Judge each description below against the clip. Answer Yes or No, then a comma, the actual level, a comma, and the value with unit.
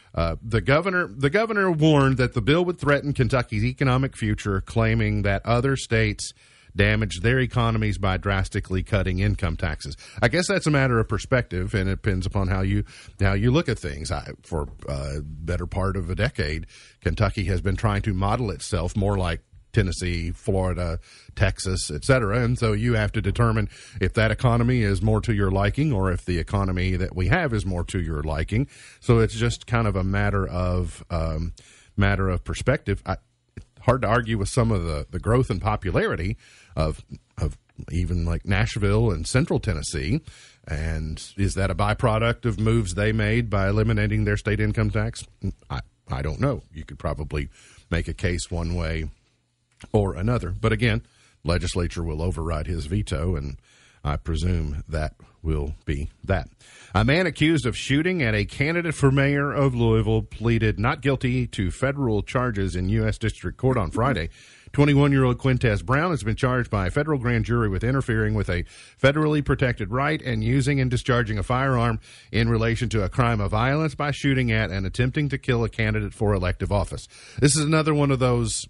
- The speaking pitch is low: Yes, low, 105 Hz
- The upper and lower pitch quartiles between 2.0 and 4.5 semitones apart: No, average, 4.9 semitones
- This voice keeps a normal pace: Yes, average, 185 wpm